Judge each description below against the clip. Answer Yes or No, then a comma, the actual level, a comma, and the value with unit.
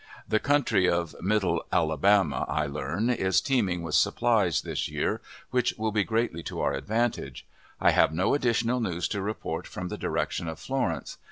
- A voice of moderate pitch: No, low, 100 Hz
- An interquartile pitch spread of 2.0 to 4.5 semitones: No, wide, 5.5 semitones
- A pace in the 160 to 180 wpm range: Yes, average, 170 wpm